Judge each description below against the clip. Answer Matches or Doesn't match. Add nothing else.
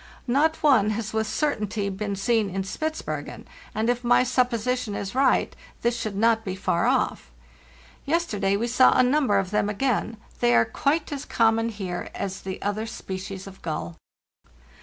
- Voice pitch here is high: Matches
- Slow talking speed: Doesn't match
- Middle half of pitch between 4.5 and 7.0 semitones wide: Doesn't match